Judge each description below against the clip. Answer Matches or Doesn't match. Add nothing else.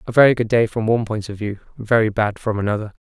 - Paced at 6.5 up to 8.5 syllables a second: Matches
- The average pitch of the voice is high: Doesn't match